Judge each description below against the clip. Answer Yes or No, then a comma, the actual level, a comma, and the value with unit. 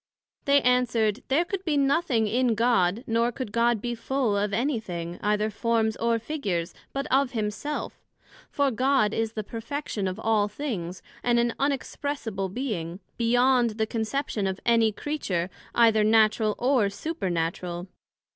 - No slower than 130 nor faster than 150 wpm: Yes, average, 145 wpm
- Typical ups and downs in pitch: Yes, average, 3.8 semitones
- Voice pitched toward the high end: Yes, high, 230 Hz